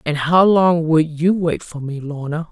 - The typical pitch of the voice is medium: Yes, medium, 160 Hz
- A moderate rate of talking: No, fast, 215 wpm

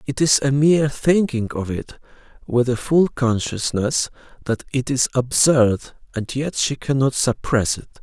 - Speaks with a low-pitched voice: Yes, low, 130 Hz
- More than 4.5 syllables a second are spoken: No, 4.2 syllables/s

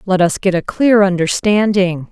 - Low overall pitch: No, high, 190 Hz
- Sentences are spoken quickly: No, average, 170 wpm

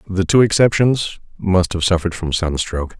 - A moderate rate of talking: Yes, average, 160 wpm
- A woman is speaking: No, male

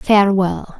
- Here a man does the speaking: No, female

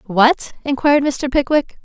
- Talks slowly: Yes, slow, 130 wpm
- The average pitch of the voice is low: No, very high, 270 Hz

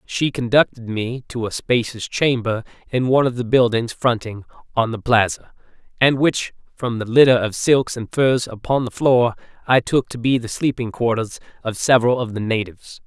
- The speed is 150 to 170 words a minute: No, average, 185 wpm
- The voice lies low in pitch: Yes, low, 120 Hz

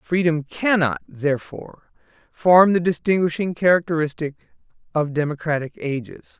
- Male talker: Yes, male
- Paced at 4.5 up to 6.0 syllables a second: Yes, 4.9 syllables/s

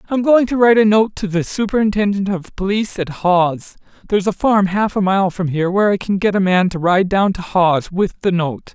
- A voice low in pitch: No, high, 195 Hz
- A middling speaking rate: No, fast, 235 wpm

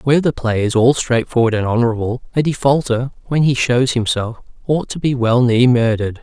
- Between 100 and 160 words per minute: No, average, 195 wpm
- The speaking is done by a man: Yes, male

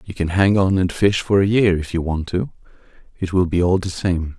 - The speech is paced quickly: Yes, fast, 260 wpm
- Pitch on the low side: Yes, very low, 90 Hz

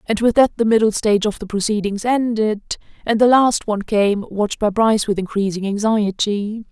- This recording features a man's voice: No, female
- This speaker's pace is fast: No, average, 180 wpm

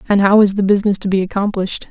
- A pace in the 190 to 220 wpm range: No, fast, 250 wpm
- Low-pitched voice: No, high, 200 Hz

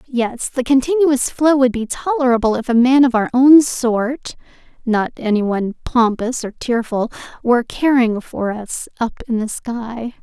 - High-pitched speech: Yes, high, 245 Hz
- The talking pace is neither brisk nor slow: Yes, average, 145 wpm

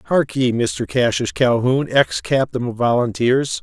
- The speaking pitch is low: Yes, low, 125 Hz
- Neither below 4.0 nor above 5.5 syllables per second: Yes, 4.1 syllables/s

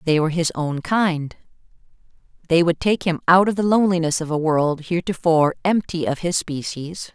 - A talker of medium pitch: Yes, medium, 170 Hz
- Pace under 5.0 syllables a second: No, 5.4 syllables/s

